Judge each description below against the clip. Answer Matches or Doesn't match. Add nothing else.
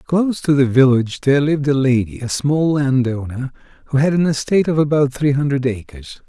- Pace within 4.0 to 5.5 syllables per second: Doesn't match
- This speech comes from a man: Matches